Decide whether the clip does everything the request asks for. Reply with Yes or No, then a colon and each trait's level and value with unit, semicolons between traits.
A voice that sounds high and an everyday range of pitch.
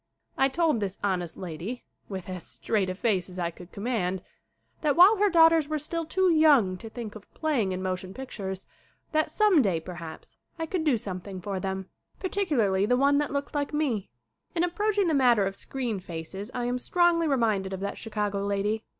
No: high, 225 Hz; wide, 8.2 semitones